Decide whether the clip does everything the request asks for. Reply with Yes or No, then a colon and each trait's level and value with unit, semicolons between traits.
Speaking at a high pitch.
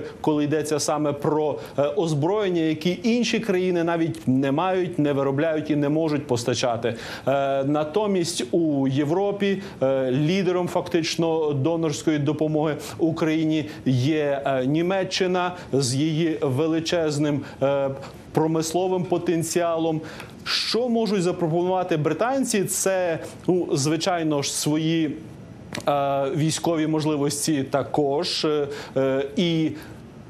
No: medium, 155 Hz